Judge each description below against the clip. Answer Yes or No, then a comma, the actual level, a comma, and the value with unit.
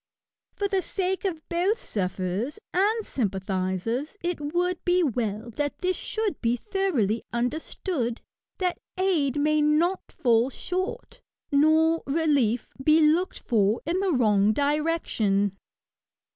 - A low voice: No, very high, 300 Hz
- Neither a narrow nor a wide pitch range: No, wide, 7.7 semitones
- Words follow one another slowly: Yes, slow, 120 wpm